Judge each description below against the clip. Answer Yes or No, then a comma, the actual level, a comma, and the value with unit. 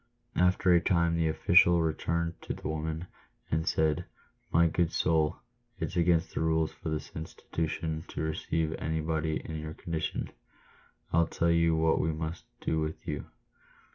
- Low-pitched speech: Yes, very low, 80 Hz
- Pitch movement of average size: No, narrow, 1.1 semitones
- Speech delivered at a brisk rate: No, average, 160 wpm